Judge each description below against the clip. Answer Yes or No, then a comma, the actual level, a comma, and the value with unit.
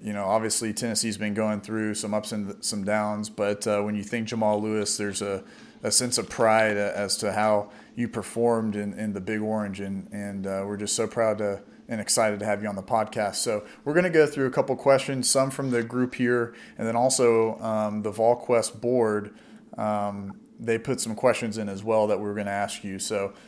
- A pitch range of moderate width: No, narrow, 2.1 semitones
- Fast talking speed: Yes, fast, 225 wpm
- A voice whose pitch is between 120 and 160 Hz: No, low, 110 Hz